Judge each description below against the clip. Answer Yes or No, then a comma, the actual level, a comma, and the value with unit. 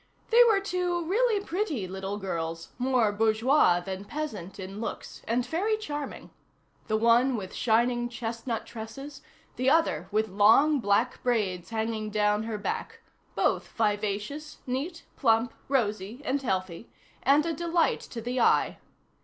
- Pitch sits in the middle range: No, high, 230 Hz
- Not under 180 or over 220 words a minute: No, average, 140 wpm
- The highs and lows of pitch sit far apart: Yes, wide, 5.8 semitones